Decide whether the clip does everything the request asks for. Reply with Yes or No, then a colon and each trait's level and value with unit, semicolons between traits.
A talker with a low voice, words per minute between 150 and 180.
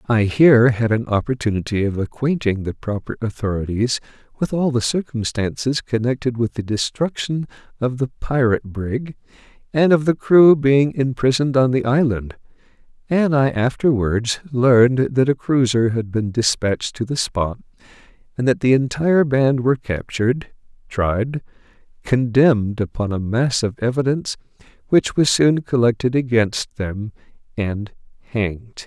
No: low, 125 Hz; slow, 135 wpm